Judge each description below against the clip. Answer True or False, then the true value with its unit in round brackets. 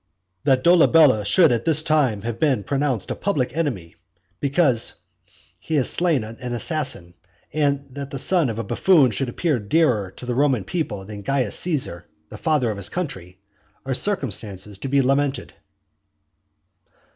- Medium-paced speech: True (155 wpm)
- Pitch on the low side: True (130 Hz)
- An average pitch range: False (5.9 semitones)